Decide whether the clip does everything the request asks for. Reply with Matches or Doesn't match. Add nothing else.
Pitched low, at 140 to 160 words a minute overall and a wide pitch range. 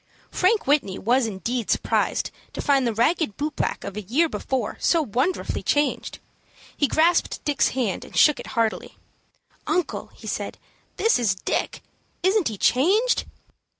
Doesn't match